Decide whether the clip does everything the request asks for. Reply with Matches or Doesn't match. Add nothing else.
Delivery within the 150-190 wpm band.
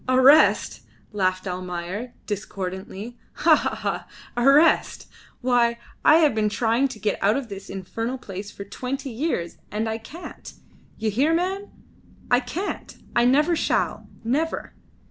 Doesn't match